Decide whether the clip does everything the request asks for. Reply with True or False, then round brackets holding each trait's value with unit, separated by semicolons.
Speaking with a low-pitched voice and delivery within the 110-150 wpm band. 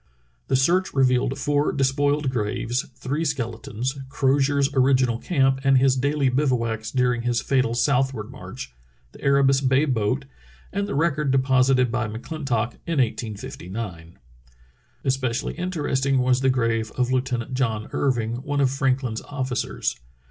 True (130 Hz; 135 wpm)